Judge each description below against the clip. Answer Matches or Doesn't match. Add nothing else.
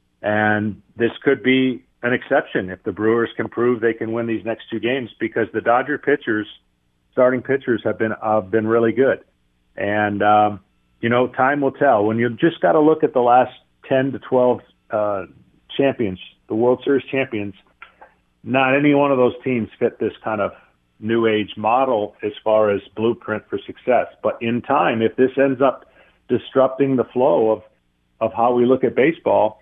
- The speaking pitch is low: Matches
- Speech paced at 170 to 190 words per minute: Matches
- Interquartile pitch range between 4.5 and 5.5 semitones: Doesn't match